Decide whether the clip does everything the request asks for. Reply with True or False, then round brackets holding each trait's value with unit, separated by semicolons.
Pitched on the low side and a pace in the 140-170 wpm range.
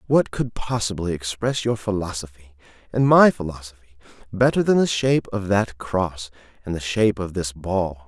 True (100 Hz; 165 wpm)